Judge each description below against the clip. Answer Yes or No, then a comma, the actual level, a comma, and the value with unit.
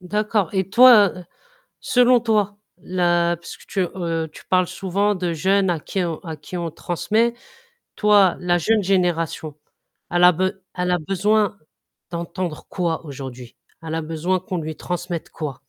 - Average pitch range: Yes, average, 3.1 semitones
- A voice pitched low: No, medium, 180 Hz